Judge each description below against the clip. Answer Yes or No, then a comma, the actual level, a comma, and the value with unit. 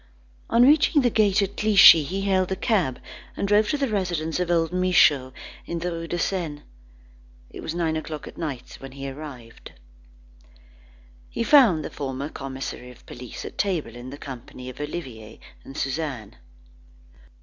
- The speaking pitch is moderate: Yes, medium, 160 Hz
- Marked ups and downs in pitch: Yes, wide, 6.0 semitones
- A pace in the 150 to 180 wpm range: Yes, average, 165 wpm